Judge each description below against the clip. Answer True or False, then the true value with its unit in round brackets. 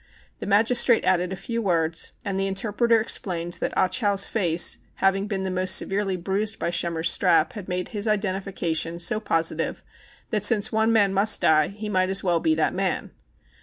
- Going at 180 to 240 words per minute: True (185 wpm)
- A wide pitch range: False (3.1 semitones)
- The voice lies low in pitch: False (195 Hz)